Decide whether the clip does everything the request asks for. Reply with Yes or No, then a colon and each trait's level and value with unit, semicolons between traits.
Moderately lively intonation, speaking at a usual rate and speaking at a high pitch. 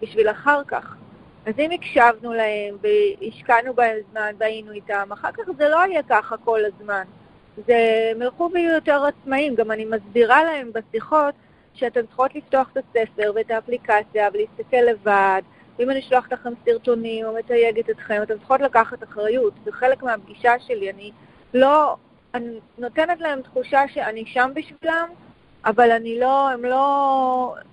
Yes: average, 3.7 semitones; average, 150 wpm; high, 240 Hz